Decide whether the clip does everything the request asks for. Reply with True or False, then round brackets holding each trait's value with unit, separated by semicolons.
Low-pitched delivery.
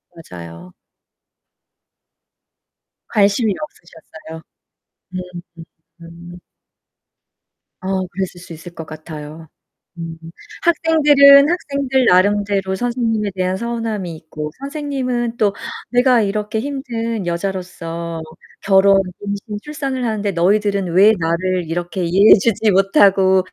False (195 Hz)